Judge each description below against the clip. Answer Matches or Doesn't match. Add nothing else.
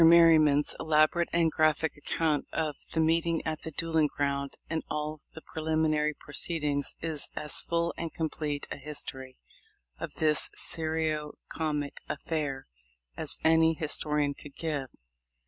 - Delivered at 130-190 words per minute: Matches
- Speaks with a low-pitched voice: Doesn't match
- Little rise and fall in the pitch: Matches